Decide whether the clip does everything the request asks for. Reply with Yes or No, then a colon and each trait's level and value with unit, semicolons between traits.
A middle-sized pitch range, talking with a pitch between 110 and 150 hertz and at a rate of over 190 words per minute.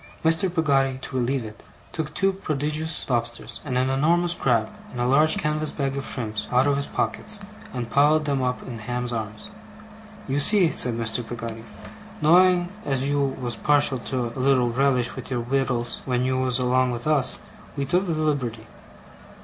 No: average, 3.6 semitones; low, 135 Hz; average, 180 wpm